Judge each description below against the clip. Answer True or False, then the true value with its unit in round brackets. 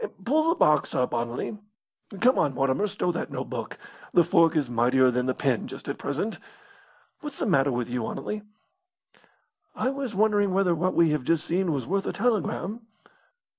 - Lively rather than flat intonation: True (8.1 semitones)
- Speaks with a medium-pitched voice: True (170 Hz)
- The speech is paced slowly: False (175 wpm)